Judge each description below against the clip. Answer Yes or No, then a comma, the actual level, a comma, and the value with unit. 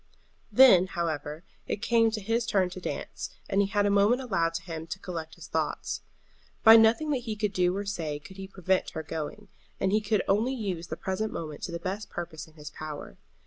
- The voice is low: No, high, 190 Hz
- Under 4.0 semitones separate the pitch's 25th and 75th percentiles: No, average, 4.3 semitones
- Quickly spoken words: Yes, fast, 220 wpm